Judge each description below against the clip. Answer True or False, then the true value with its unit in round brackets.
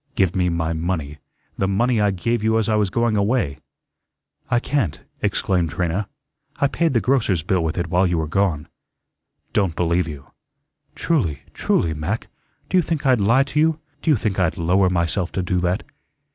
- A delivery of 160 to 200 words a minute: True (185 wpm)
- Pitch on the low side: True (95 Hz)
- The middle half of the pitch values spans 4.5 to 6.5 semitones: True (5.5 semitones)